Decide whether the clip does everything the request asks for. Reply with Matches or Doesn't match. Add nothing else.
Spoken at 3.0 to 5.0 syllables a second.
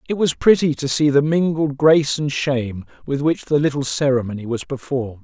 Doesn't match